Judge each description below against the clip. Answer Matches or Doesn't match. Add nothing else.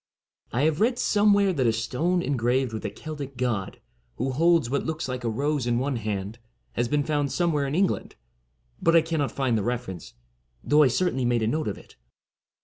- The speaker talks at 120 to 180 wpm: Doesn't match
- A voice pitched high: Doesn't match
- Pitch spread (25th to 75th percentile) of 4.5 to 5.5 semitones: Matches